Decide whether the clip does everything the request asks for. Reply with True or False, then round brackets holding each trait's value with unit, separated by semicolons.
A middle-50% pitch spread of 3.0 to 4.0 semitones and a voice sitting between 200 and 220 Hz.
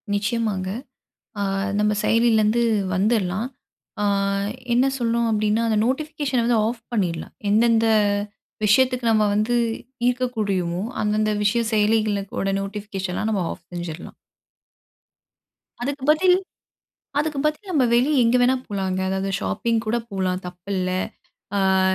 True (3.5 semitones; 215 Hz)